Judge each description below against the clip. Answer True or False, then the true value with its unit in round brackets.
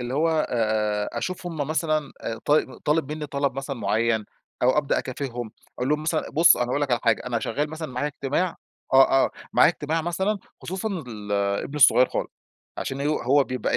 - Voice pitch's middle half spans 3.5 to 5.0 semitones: True (3.8 semitones)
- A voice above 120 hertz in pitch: True (140 Hz)